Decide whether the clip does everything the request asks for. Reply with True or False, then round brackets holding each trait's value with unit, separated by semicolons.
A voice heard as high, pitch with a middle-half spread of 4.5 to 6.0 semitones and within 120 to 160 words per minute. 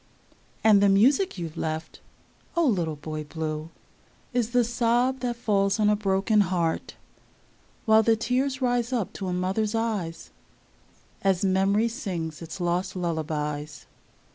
True (195 Hz; 5.5 semitones; 140 wpm)